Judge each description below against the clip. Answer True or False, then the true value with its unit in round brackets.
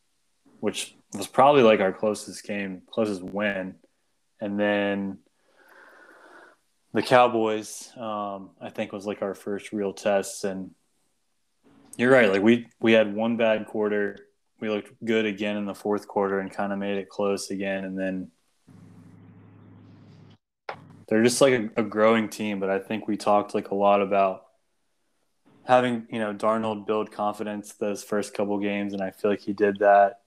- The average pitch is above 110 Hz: False (105 Hz)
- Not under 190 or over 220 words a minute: False (165 wpm)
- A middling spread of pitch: False (1.8 semitones)